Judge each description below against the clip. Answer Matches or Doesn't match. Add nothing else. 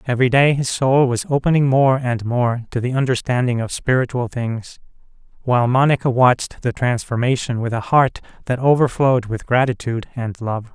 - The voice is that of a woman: Doesn't match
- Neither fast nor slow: Matches